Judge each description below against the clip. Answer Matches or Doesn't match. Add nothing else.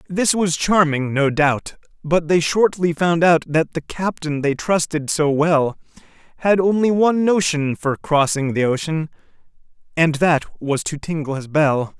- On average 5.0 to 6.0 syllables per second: Doesn't match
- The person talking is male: Matches